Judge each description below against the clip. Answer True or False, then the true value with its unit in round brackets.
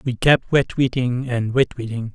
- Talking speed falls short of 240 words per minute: True (140 wpm)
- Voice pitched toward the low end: True (125 Hz)